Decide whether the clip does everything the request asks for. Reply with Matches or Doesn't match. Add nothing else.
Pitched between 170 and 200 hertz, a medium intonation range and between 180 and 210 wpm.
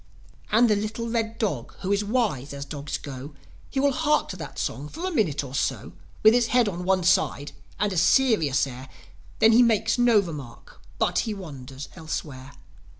Doesn't match